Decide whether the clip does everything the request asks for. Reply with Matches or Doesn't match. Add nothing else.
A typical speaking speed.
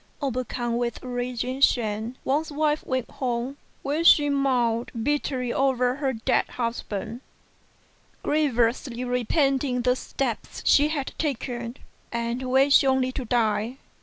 Doesn't match